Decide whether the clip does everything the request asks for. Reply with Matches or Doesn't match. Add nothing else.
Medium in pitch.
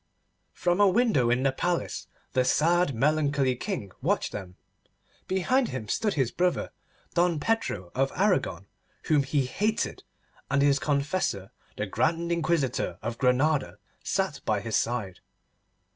Matches